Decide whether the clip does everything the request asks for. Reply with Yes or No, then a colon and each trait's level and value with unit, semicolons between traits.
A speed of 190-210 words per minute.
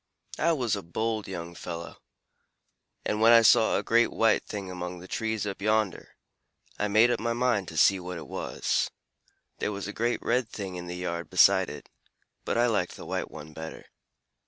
Yes: average, 195 wpm